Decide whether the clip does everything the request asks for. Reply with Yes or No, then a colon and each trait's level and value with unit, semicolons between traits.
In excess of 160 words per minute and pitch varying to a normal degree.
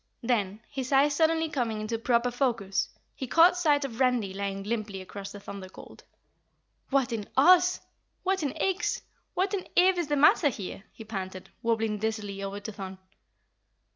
No: average, 170 wpm; wide, 6.4 semitones